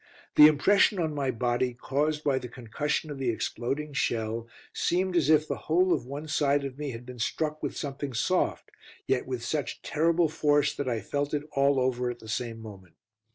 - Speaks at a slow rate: No, average, 200 wpm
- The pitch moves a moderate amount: Yes, average, 3.7 semitones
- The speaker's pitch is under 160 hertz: Yes, medium, 140 Hz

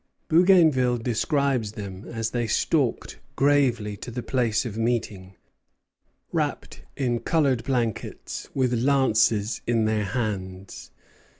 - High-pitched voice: No, low, 120 Hz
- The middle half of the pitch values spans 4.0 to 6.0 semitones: No, average, 3.4 semitones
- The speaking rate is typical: No, slow, 110 wpm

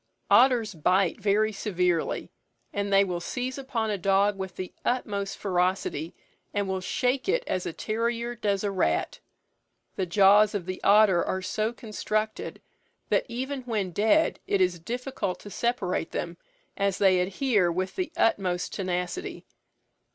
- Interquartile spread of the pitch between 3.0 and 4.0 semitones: Yes, average, 3.7 semitones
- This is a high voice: Yes, high, 200 Hz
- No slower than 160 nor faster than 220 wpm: No, average, 150 wpm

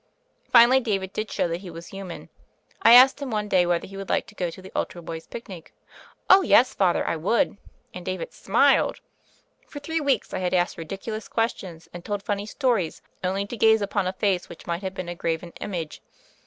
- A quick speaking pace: Yes, fast, 210 wpm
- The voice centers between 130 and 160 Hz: No, high, 195 Hz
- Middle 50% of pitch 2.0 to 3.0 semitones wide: No, average, 4.1 semitones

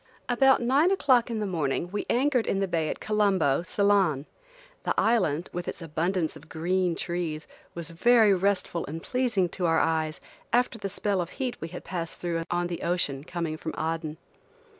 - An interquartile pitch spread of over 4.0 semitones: Yes, average, 4.4 semitones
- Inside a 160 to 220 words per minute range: Yes, average, 180 wpm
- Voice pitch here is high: No, medium, 180 Hz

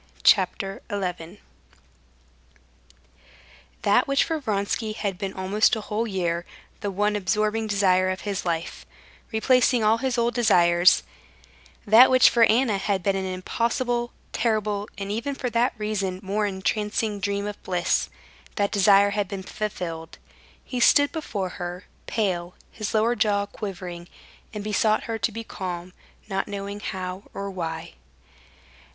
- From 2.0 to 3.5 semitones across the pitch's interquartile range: Yes, average, 2.9 semitones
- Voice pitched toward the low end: No, high, 205 Hz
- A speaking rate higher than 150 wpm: No, average, 140 wpm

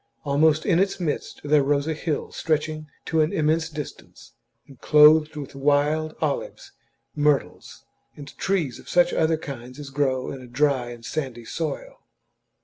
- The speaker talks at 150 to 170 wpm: Yes, average, 155 wpm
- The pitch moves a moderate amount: No, narrow, 2.2 semitones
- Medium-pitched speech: Yes, medium, 150 Hz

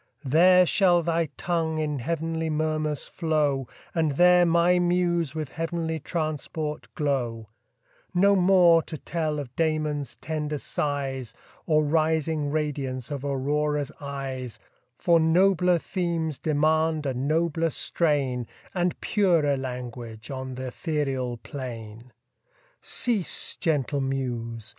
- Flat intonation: No, average, 3.6 semitones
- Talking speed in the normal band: No, slow, 115 wpm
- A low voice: No, medium, 155 Hz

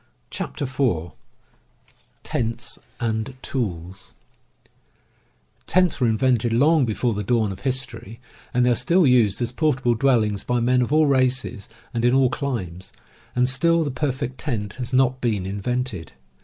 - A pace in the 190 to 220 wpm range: No, average, 160 wpm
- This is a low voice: Yes, low, 125 Hz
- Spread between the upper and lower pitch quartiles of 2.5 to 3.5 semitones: Yes, average, 3.2 semitones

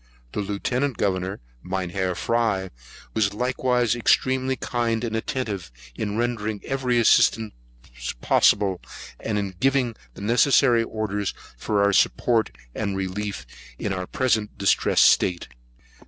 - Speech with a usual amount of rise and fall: Yes, average, 3.4 semitones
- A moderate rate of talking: No, slow, 120 wpm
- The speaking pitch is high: No, low, 110 Hz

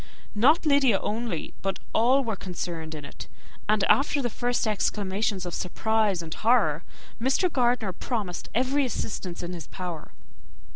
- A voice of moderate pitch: No, high, 215 Hz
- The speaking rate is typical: Yes, average, 150 wpm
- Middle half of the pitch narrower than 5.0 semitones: No, wide, 5.4 semitones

